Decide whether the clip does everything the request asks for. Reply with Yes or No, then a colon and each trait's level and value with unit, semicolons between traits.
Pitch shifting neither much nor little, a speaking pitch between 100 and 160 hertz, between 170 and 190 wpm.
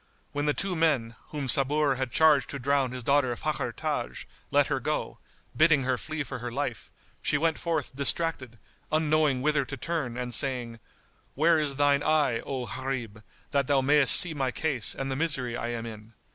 Yes: average, 3.5 semitones; medium, 140 Hz; average, 185 wpm